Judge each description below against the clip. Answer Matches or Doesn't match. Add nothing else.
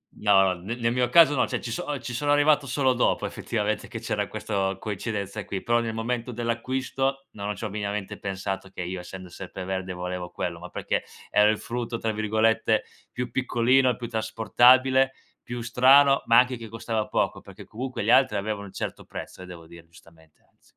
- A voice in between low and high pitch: Doesn't match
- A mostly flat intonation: Doesn't match